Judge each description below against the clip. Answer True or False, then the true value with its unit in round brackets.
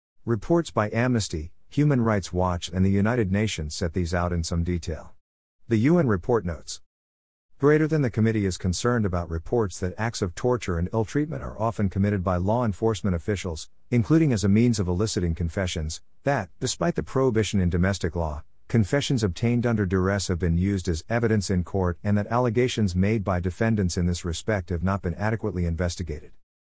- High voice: False (100 Hz)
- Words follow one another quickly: False (185 wpm)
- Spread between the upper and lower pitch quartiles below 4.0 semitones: False (4.4 semitones)